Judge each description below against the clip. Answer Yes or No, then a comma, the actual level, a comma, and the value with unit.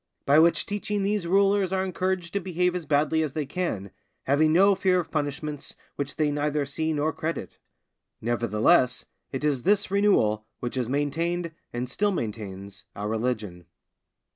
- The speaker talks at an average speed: Yes, average, 160 wpm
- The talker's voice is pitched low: No, medium, 155 Hz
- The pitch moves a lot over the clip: Yes, wide, 6.3 semitones